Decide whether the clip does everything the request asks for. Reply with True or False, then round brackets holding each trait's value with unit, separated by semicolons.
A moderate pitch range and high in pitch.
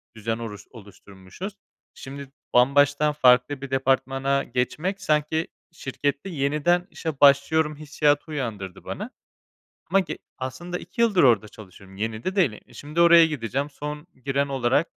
False (3.9 semitones; 140 Hz)